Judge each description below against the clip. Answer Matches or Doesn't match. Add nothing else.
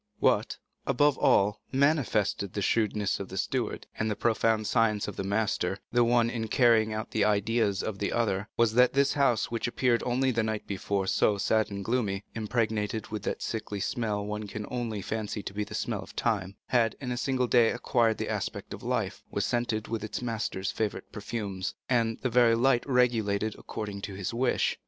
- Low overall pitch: Matches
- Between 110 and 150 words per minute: Doesn't match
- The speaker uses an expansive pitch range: Doesn't match